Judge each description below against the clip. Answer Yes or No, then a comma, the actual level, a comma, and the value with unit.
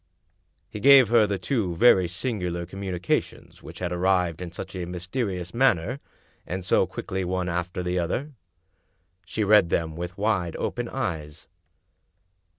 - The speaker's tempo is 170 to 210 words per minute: No, average, 145 wpm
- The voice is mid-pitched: No, very low, 90 Hz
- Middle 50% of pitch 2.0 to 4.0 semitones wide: Yes, average, 3.0 semitones